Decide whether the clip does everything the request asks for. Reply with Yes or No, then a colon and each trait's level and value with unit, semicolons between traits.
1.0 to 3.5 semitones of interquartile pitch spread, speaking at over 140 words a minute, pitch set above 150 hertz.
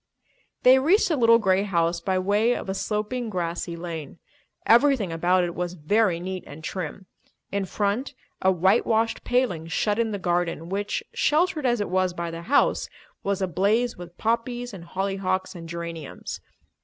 No: average, 4.6 semitones; average, 170 wpm; high, 190 Hz